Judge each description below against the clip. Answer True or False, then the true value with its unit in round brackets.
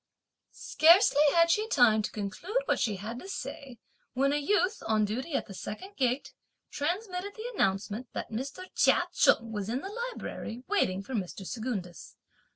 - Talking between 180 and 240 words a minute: False (165 wpm)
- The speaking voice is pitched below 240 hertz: False (255 Hz)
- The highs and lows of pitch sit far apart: True (8.9 semitones)